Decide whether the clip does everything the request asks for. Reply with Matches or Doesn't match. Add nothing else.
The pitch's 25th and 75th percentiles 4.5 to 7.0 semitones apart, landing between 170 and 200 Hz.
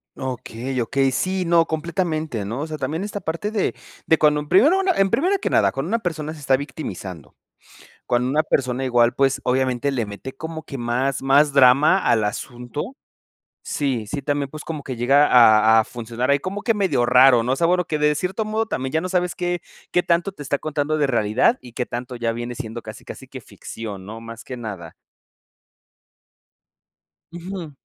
Doesn't match